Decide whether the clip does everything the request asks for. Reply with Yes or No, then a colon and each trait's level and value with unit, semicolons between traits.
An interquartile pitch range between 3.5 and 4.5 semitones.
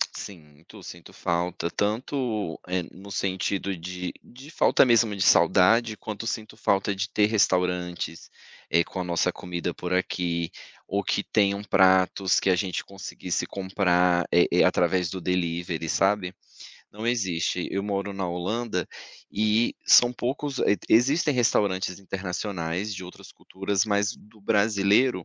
No: average, 3.0 semitones